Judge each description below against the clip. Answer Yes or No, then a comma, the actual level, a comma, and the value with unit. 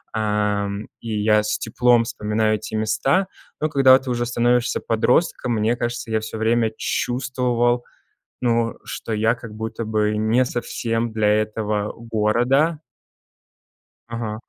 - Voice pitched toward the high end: No, low, 115 Hz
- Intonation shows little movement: Yes, narrow, 2.0 semitones